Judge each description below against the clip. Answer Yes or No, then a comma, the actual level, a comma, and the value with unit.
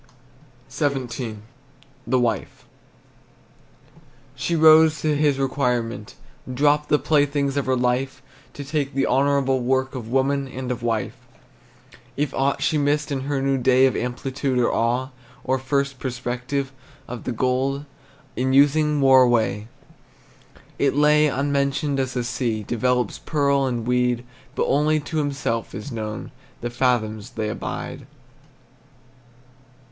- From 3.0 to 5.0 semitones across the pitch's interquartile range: No, narrow, 2.4 semitones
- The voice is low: Yes, low, 130 Hz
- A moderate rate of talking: No, slow, 130 wpm